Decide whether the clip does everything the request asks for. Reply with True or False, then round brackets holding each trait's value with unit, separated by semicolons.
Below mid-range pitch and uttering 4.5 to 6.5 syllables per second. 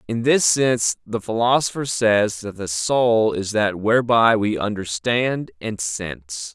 False (105 Hz; 4.0 syllables/s)